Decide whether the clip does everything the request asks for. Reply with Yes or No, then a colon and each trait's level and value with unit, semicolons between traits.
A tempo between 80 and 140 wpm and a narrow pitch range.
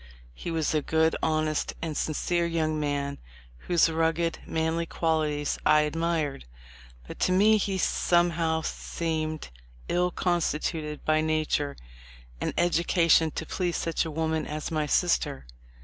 Yes: slow, 135 wpm; narrow, 1.6 semitones